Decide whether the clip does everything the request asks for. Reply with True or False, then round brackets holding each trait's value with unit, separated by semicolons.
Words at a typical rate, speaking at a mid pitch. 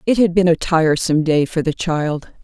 False (220 wpm; 165 Hz)